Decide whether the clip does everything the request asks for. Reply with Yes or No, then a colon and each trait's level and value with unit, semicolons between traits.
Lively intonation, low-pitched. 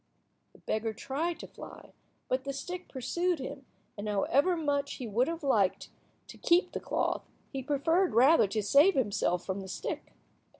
No: wide, 7.1 semitones; very high, 275 Hz